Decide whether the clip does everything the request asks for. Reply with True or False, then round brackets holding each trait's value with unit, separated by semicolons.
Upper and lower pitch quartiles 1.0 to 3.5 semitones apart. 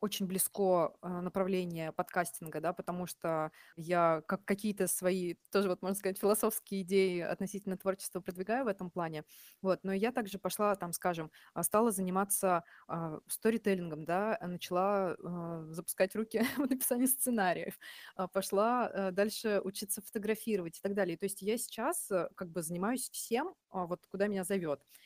True (2.8 semitones)